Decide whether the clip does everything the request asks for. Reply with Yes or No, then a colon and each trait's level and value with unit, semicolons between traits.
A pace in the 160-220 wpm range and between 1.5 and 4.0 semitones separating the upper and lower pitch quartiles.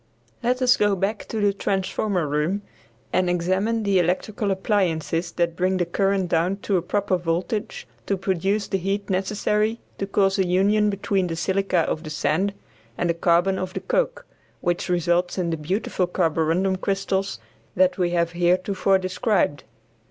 Yes: average, 165 wpm; narrow, 2.4 semitones